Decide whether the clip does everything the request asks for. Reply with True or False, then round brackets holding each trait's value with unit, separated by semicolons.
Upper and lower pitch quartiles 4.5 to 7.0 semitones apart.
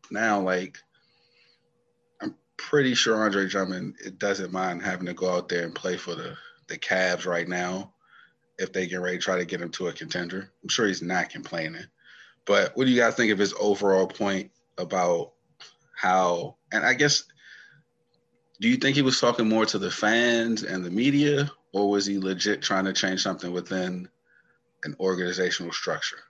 False (3.4 semitones)